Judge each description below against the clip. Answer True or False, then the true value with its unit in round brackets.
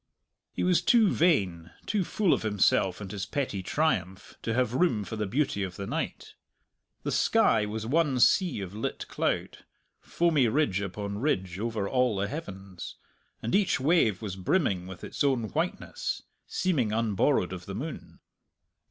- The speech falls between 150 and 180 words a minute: True (160 wpm)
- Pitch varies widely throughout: True (7.2 semitones)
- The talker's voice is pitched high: False (110 Hz)